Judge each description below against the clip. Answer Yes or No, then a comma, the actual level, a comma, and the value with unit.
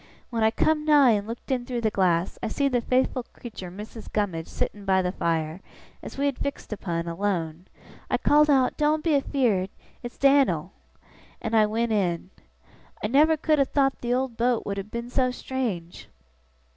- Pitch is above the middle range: Yes, high, 230 Hz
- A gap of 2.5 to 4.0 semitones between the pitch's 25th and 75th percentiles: No, wide, 5.6 semitones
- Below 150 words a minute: No, average, 185 wpm